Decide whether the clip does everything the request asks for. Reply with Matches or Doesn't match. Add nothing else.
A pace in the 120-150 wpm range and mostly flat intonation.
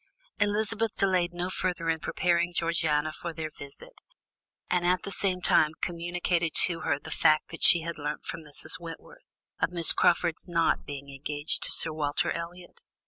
Doesn't match